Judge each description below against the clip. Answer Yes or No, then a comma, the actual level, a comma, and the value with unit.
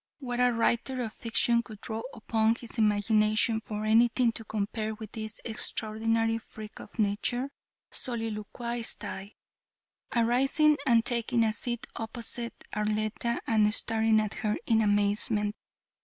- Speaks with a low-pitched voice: No, high, 225 Hz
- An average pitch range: No, narrow, 1.7 semitones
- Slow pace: Yes, slow, 125 wpm